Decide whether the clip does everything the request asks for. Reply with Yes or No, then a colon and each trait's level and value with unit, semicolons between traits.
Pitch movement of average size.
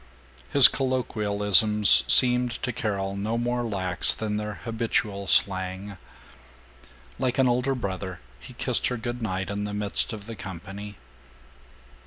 Yes: average, 3.4 semitones